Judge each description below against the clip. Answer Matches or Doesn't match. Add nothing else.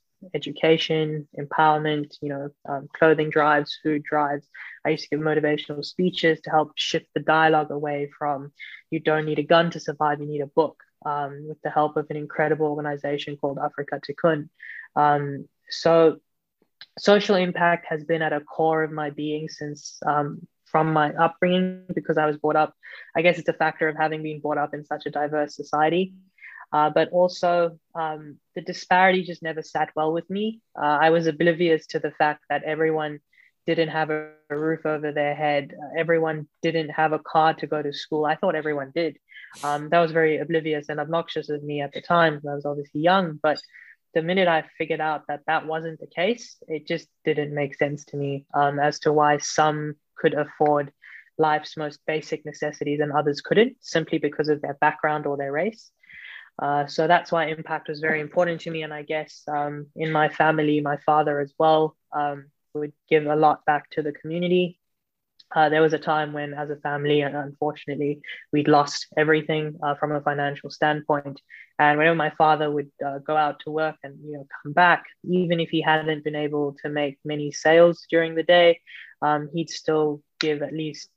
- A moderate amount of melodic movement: Doesn't match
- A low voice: Doesn't match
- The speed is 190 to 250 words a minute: Matches